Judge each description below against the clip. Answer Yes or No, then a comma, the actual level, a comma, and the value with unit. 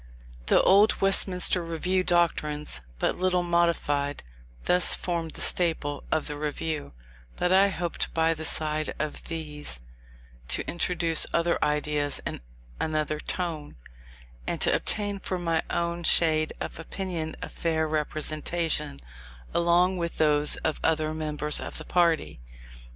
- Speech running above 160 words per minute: No, slow, 135 wpm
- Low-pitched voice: No, medium, 160 Hz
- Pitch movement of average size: No, narrow, 2.3 semitones